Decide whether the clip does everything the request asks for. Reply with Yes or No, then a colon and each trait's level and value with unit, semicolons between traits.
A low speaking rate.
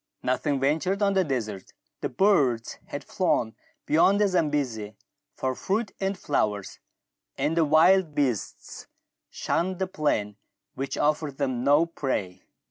Yes: slow, 130 wpm